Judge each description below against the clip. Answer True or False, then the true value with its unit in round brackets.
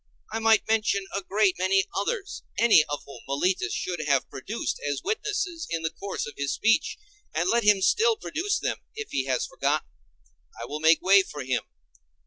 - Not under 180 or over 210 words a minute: True (185 wpm)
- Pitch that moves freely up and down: True (7.4 semitones)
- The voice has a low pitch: False (195 Hz)